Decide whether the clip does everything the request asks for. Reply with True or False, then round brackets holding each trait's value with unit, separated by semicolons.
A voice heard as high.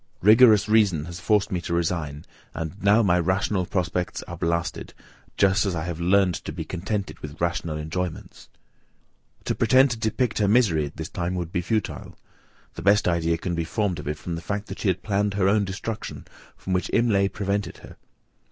False (95 Hz)